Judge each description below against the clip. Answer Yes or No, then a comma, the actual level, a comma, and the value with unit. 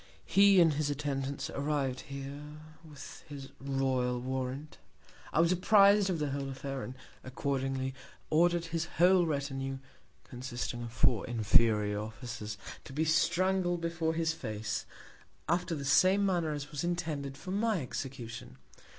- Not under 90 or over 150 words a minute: Yes, average, 140 wpm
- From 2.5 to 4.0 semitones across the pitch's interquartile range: No, average, 4.4 semitones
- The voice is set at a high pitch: No, medium, 140 Hz